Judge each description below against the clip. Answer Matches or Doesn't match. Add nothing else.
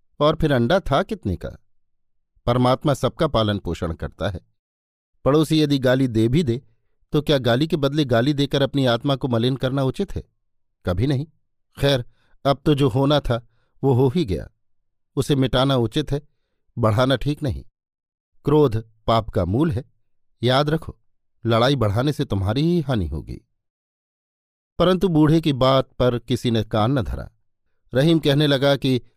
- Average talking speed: Matches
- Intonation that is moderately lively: Matches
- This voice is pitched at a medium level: Doesn't match